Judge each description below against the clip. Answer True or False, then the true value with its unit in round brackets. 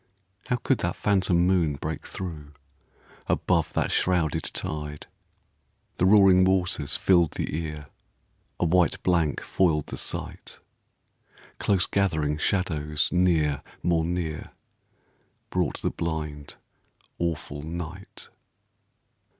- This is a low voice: True (85 Hz)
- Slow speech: True (105 wpm)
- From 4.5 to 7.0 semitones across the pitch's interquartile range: False (3.2 semitones)